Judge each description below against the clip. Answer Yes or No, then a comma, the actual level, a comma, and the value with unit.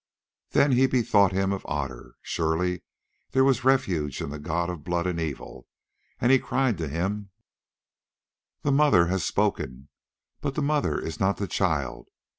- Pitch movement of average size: No, wide, 7.9 semitones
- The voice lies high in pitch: No, very low, 95 Hz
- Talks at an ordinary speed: Yes, average, 160 wpm